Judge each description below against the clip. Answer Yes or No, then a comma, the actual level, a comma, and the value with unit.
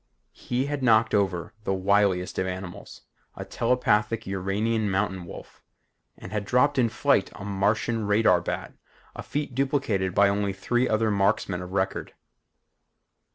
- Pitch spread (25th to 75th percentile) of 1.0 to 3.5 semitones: Yes, average, 3.0 semitones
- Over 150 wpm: No, average, 145 wpm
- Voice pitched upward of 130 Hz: No, low, 105 Hz